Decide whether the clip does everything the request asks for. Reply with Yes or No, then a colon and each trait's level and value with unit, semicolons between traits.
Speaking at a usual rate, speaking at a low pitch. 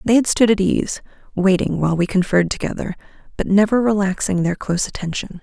No: average, 175 wpm; high, 195 Hz